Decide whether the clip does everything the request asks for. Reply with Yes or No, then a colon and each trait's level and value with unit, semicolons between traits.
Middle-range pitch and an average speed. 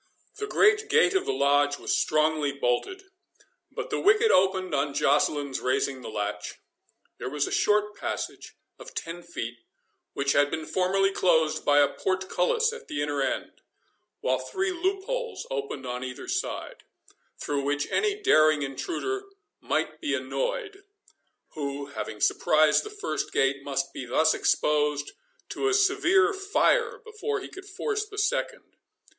Yes: medium, 180 Hz; average, 150 wpm